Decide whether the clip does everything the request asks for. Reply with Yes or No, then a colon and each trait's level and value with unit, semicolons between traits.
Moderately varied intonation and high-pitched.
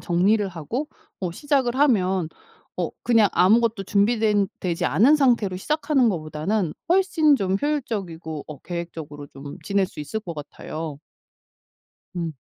No: wide, 6.2 semitones; high, 195 Hz